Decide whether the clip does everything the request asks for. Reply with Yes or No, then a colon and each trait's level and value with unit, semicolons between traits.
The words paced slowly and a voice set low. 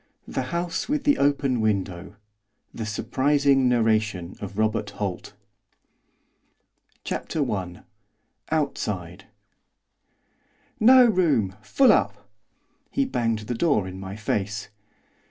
Yes: slow, 100 wpm; low, 110 Hz